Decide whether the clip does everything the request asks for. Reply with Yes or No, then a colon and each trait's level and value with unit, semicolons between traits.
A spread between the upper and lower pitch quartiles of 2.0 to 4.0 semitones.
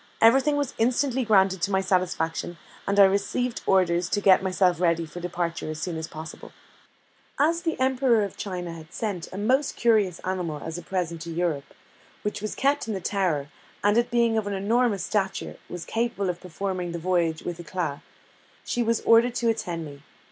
No: average, 4.8 semitones